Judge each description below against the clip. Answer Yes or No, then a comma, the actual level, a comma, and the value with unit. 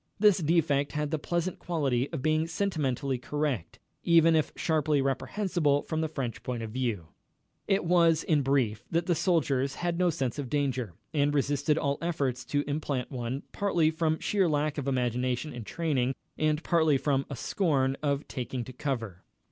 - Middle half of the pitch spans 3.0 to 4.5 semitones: Yes, average, 3.6 semitones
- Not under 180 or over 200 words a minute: No, average, 170 wpm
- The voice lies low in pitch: No, medium, 145 Hz